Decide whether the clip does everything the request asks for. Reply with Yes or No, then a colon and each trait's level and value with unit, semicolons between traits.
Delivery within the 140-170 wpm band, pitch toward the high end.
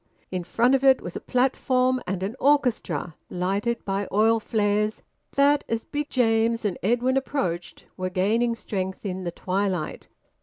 Yes: average, 155 wpm; high, 220 Hz